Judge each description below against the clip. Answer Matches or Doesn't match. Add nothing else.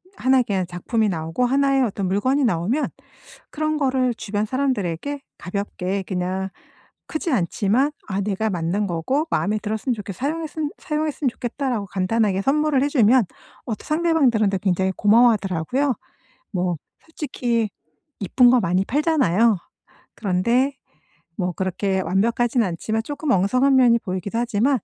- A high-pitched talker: Matches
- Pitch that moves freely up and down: Matches